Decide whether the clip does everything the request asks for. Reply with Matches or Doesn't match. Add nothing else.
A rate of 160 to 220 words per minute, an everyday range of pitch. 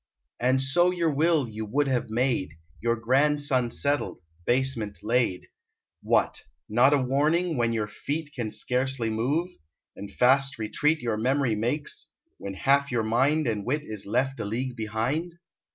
Doesn't match